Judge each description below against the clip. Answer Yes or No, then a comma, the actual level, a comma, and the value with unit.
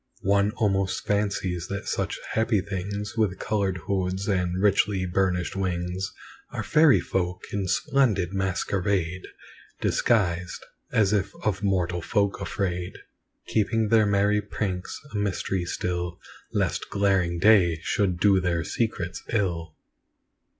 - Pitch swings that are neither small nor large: No, narrow, 2.3 semitones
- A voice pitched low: Yes, very low, 95 Hz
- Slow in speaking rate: Yes, slow, 120 wpm